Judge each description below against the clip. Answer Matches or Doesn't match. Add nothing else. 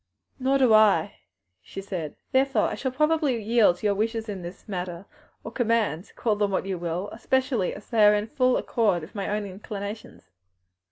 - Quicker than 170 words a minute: Matches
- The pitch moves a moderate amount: Matches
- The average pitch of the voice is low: Doesn't match